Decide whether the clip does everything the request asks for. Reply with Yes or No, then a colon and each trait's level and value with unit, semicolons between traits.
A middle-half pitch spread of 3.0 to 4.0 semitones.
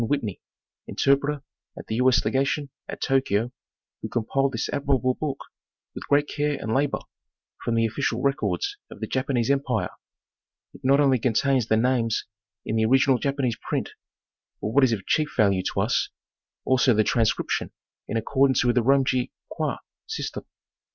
Yes: average, 3.3 semitones